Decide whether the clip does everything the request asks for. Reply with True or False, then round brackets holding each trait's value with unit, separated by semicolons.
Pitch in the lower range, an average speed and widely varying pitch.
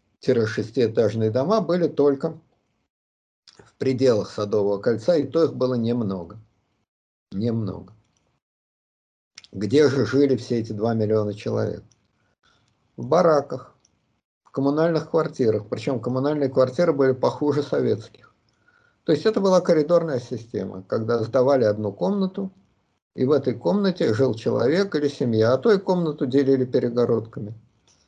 True (125 Hz; 120 wpm; 5.8 semitones)